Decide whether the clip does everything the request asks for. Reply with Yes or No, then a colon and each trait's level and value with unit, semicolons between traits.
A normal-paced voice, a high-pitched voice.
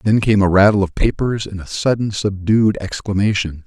No: average, 180 wpm; low, 100 Hz